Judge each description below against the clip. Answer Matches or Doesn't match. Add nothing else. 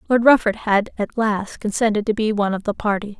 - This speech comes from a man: Doesn't match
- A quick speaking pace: Matches